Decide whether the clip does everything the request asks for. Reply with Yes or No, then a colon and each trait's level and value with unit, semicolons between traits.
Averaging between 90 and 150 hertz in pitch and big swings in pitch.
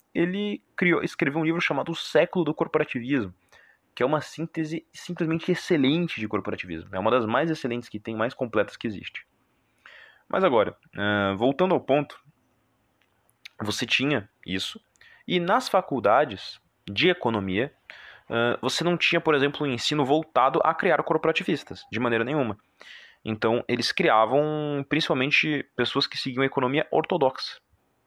Yes: medium, 140 Hz; wide, 5.9 semitones